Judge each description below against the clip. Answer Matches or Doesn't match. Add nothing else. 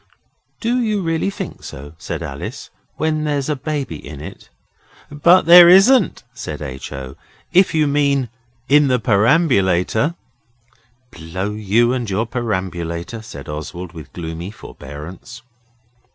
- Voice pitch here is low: Matches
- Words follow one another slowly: Matches